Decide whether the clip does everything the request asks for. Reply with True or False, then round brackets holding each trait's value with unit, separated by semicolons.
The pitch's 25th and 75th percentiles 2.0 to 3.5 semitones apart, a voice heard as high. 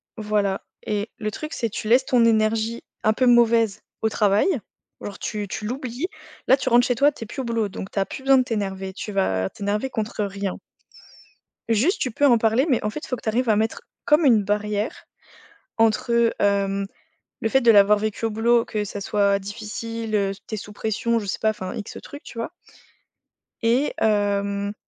True (2.5 semitones; 220 Hz)